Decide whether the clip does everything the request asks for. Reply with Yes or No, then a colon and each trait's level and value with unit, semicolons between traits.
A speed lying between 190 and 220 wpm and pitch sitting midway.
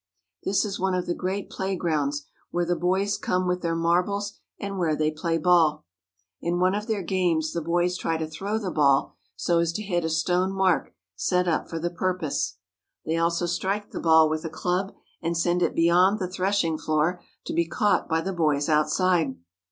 Yes: average, 200 wpm; medium, 175 Hz